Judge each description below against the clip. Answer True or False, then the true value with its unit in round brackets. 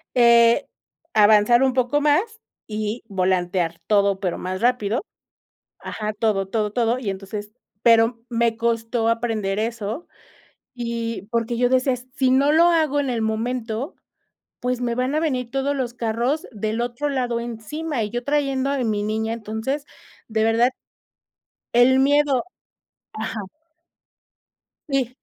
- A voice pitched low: False (235 Hz)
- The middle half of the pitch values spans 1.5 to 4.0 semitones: True (3.0 semitones)